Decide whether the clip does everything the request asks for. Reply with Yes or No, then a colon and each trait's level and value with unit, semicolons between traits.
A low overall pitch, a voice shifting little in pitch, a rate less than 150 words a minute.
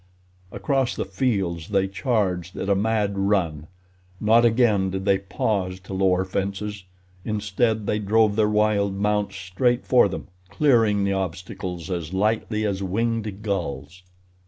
Yes: low, 100 Hz; narrow, 2.3 semitones; average, 140 wpm